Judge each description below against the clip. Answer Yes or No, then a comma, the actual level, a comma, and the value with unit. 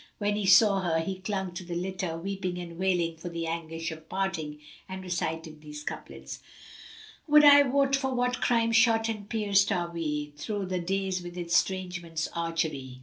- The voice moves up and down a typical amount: Yes, average, 3.6 semitones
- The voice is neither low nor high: Yes, medium, 180 Hz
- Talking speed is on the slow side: No, average, 180 wpm